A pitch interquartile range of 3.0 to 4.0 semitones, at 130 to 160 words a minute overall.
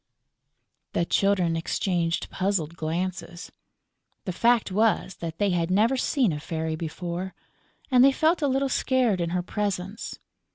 No: average, 4.7 semitones; average, 140 wpm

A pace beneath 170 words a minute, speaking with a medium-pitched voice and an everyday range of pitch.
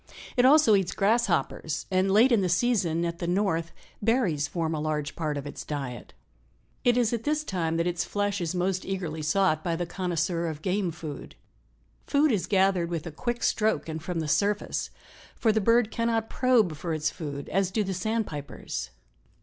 No: average, 190 wpm; medium, 180 Hz; average, 4.9 semitones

